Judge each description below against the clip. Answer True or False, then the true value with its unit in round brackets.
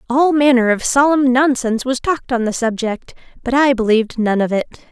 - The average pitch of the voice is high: True (250 Hz)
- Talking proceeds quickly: False (195 wpm)